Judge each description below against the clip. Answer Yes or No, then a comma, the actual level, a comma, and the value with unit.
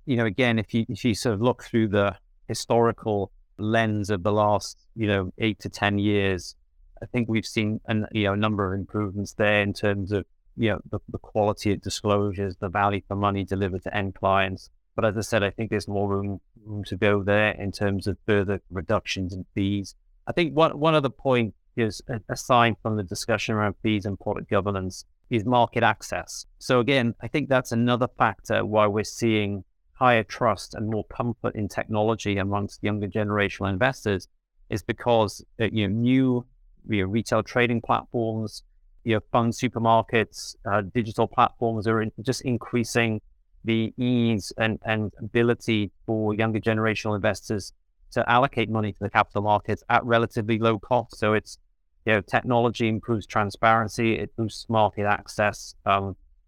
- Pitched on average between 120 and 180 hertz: No, low, 105 Hz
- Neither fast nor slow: Yes, average, 175 wpm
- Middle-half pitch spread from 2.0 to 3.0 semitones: Yes, narrow, 2.5 semitones